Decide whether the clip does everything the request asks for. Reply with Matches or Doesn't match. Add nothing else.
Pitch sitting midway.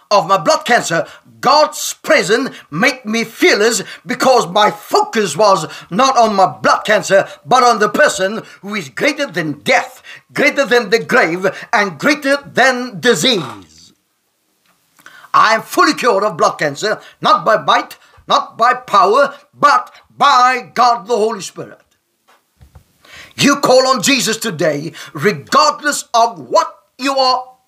Doesn't match